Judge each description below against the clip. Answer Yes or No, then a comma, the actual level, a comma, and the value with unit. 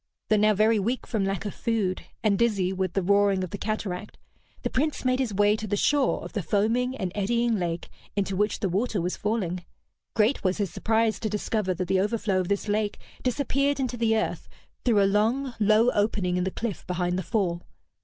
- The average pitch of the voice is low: No, high, 210 Hz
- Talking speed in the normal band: No, fast, 210 wpm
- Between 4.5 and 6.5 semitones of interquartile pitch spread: No, average, 3.2 semitones